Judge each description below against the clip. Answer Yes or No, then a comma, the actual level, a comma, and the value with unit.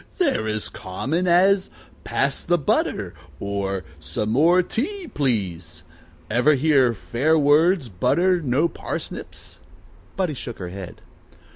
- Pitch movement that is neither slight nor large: No, wide, 8.7 semitones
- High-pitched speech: No, medium, 140 Hz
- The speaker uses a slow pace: Yes, slow, 120 wpm